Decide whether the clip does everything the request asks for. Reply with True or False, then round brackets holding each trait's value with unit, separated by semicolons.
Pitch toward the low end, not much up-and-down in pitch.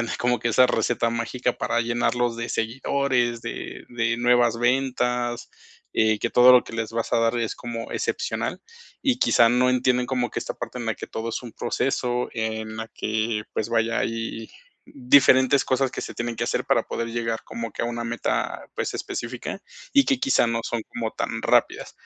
True (120 Hz; 1.3 semitones)